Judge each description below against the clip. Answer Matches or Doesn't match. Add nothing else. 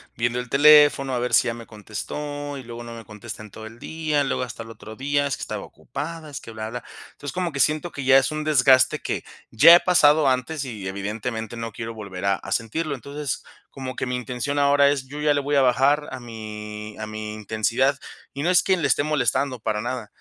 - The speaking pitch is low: Matches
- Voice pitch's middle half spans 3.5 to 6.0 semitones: Matches